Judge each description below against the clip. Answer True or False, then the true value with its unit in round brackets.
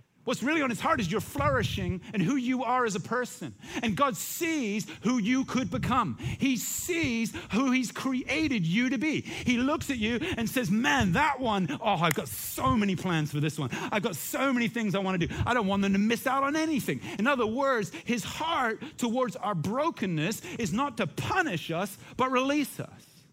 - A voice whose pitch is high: True (235 Hz)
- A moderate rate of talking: False (210 wpm)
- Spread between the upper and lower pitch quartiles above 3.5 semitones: True (4.8 semitones)